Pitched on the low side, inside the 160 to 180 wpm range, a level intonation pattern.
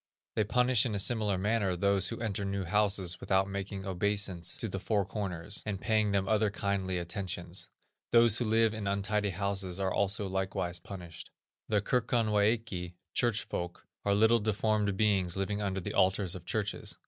Yes: low, 100 Hz; average, 170 wpm; narrow, 2.1 semitones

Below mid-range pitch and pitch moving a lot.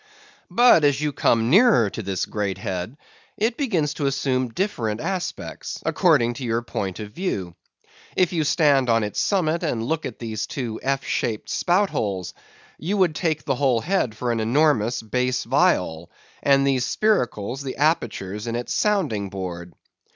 Yes: low, 130 Hz; wide, 6.5 semitones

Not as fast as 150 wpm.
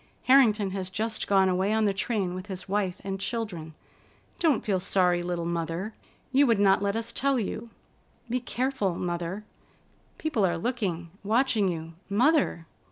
No: average, 160 wpm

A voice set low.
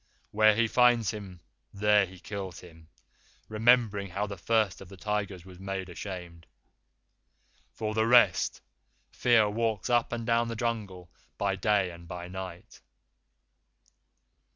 Yes: low, 100 Hz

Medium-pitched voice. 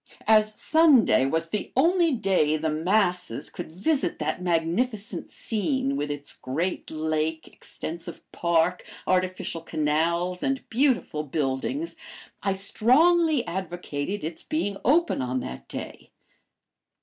Yes: medium, 180 Hz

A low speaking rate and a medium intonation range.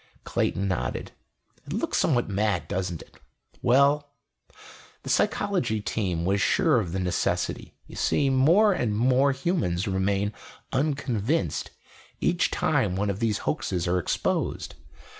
No: slow, 130 wpm; wide, 6.4 semitones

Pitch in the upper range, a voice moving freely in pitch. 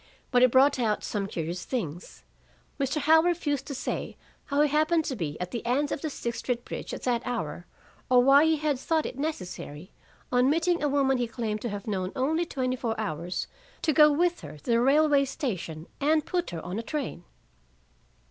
Yes: very high, 260 Hz; wide, 5.8 semitones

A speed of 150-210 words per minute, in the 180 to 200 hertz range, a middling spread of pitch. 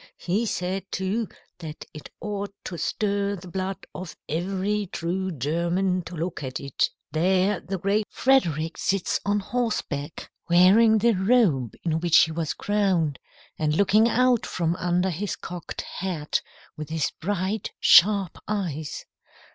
No: average, 140 wpm; medium, 185 Hz; average, 3.6 semitones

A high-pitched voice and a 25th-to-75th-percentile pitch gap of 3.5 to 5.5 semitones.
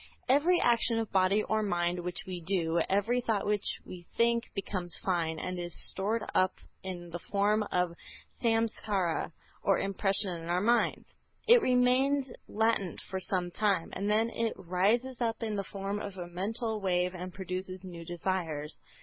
Yes: high, 195 Hz; average, 3.9 semitones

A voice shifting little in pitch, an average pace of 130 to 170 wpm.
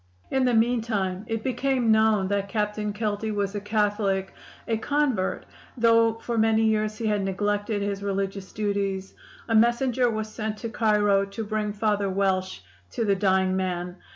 Yes: narrow, 2.2 semitones; average, 160 wpm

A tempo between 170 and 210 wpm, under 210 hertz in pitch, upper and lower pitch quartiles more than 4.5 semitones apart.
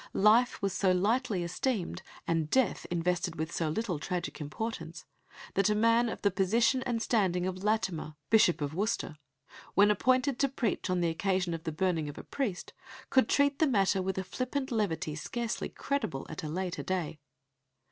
Yes: average, 180 wpm; high, 190 Hz; average, 5.1 semitones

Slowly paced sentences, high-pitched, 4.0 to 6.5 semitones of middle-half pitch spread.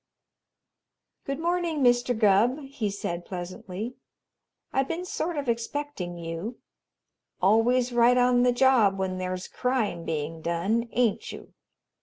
Yes: slow, 125 wpm; high, 235 Hz; wide, 5.6 semitones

